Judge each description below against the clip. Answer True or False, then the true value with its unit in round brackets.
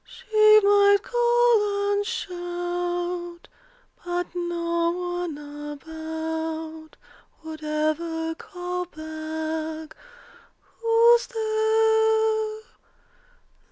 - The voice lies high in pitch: True (350 Hz)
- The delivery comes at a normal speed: False (65 wpm)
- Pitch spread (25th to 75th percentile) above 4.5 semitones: True (5.0 semitones)